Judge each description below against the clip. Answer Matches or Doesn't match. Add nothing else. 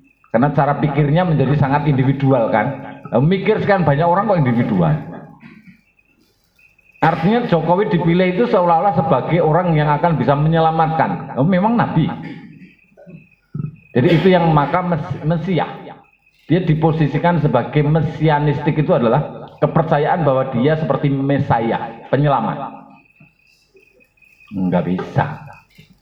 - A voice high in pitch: Doesn't match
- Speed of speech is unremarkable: Matches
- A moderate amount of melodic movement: Matches